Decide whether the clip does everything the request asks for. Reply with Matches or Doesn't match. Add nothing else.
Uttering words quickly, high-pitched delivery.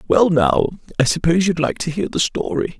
Doesn't match